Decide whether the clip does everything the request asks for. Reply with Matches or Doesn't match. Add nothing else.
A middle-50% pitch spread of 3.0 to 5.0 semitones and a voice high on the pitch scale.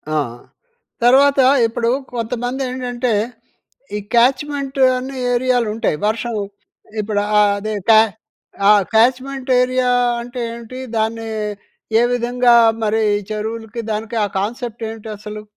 Doesn't match